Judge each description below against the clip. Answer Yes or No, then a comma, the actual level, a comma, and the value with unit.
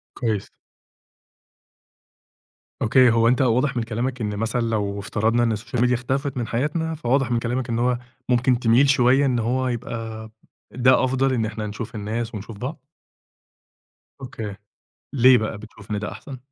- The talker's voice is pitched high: No, low, 120 Hz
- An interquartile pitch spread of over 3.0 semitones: No, narrow, 2.5 semitones